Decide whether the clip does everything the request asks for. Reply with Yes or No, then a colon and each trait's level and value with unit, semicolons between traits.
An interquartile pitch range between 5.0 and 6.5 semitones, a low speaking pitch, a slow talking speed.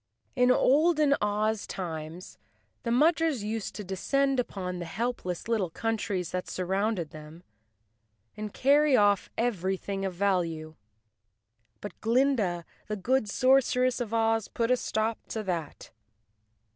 No: average, 5.3 semitones; high, 215 Hz; slow, 125 wpm